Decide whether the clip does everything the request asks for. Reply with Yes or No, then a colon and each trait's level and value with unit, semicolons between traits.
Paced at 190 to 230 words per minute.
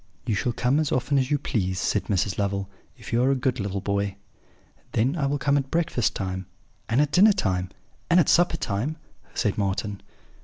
Yes: average, 200 wpm